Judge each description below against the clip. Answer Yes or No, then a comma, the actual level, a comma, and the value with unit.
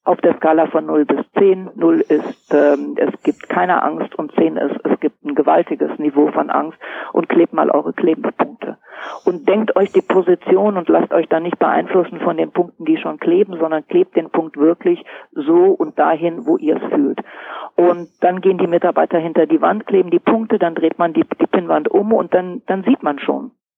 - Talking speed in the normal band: No, fast, 205 wpm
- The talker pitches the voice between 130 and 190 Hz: Yes, medium, 185 Hz